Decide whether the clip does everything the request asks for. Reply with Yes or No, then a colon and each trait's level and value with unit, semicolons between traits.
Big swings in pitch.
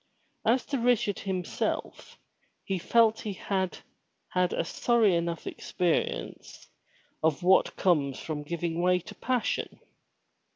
No: average, 4.3 semitones